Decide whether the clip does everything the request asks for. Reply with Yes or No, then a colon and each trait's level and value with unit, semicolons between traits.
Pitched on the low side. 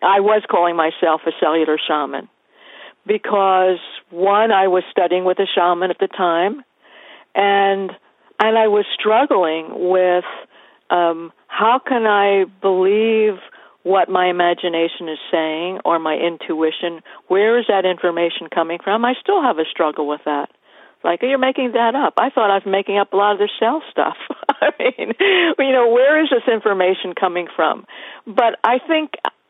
No: high, 195 Hz